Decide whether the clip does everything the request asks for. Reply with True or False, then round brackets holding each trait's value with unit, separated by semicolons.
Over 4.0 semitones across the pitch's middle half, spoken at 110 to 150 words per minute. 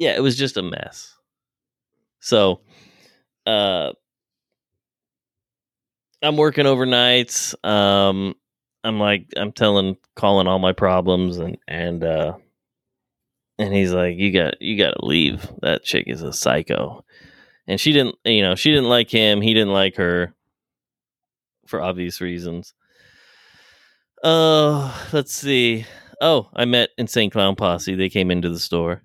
True (5.3 semitones; 140 wpm)